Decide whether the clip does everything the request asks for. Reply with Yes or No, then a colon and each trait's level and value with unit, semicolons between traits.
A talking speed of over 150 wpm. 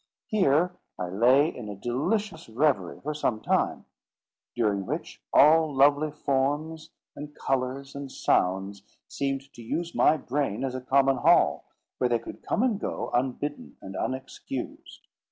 No: average, 145 wpm